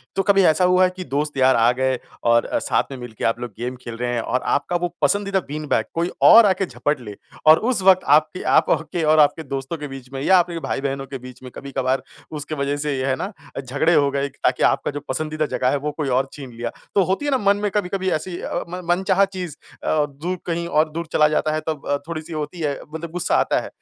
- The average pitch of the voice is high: No, medium, 150 Hz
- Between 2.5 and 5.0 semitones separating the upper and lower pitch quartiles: Yes, average, 4.7 semitones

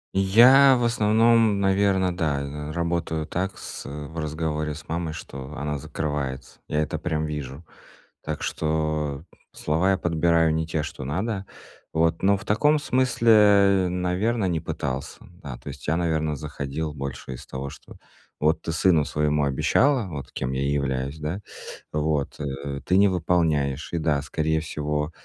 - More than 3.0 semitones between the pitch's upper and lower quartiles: Yes, average, 4.3 semitones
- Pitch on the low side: Yes, very low, 80 Hz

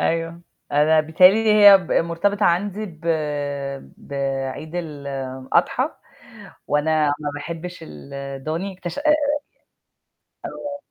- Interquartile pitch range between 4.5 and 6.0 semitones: Yes, average, 5.2 semitones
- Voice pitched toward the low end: No, medium, 165 Hz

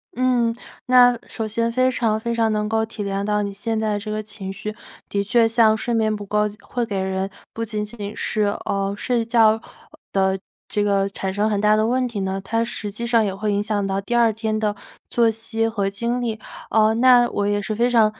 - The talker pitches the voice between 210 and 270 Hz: Yes, high, 215 Hz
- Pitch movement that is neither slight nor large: No, narrow, 2.1 semitones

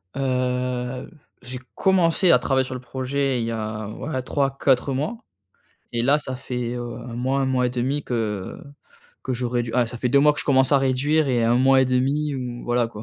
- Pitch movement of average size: No, narrow, 2.0 semitones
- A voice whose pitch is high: No, low, 130 Hz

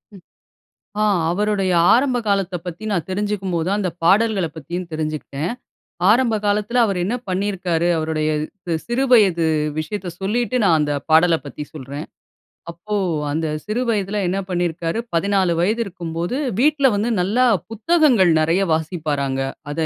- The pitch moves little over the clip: No, average, 4.4 semitones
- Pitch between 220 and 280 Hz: No, medium, 185 Hz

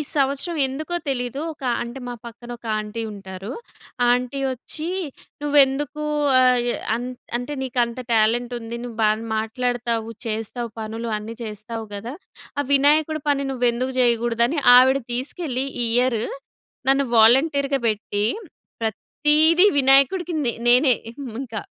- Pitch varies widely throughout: No, average, 3.2 semitones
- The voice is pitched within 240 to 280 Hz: Yes, high, 245 Hz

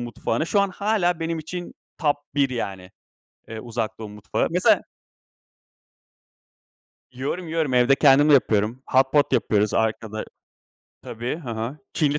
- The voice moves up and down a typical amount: No, wide, 6.0 semitones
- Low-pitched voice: Yes, low, 130 Hz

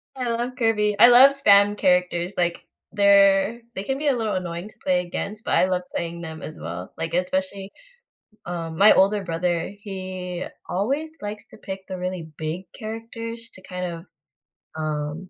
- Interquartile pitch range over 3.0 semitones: Yes, average, 3.5 semitones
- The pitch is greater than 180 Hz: Yes, high, 190 Hz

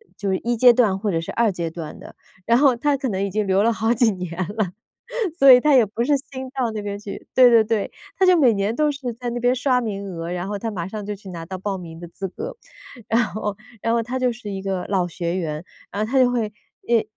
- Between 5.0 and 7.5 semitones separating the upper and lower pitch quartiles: No, average, 4.2 semitones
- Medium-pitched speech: No, high, 215 Hz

